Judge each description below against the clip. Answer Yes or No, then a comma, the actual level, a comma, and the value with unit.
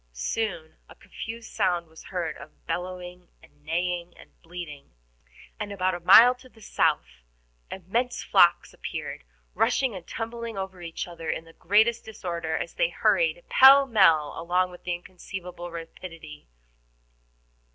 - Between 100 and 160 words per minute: Yes, average, 140 wpm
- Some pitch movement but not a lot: Yes, average, 4.7 semitones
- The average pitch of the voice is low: No, medium, 180 Hz